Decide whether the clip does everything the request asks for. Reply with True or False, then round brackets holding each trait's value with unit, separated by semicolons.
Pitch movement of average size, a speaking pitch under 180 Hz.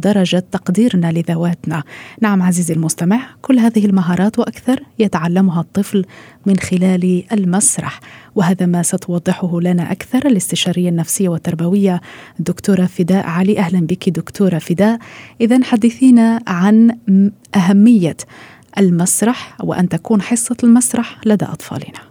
False (3.6 semitones; 190 Hz)